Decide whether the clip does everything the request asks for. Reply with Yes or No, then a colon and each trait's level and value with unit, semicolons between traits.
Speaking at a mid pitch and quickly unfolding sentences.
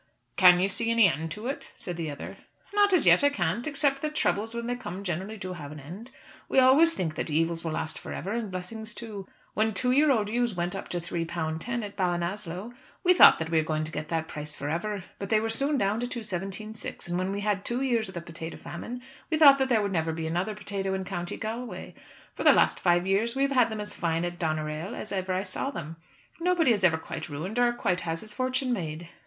No: high, 195 Hz; fast, 250 wpm